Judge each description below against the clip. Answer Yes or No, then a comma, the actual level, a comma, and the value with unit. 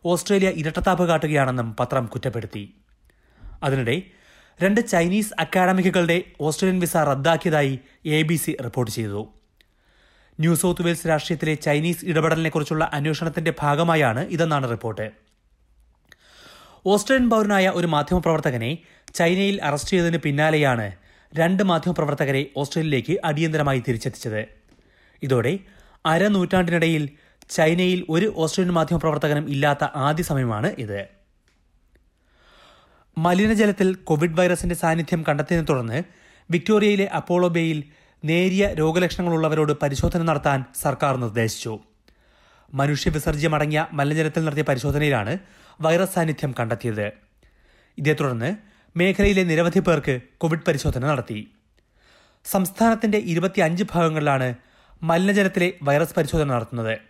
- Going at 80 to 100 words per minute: Yes, average, 90 wpm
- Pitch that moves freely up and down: No, average, 4.3 semitones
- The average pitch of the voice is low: No, medium, 160 Hz